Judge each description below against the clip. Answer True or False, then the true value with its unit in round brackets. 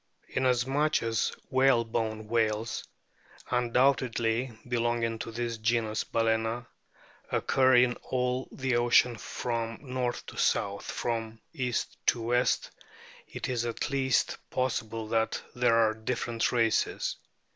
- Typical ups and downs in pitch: False (1.8 semitones)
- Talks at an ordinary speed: False (115 wpm)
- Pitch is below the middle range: True (120 Hz)